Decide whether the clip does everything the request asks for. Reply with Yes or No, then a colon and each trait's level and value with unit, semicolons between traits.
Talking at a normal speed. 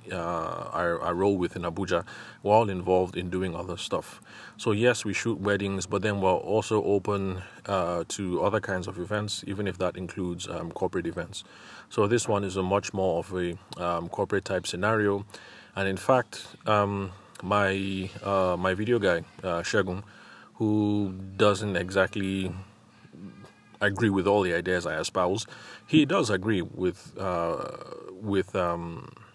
Yes: average, 155 wpm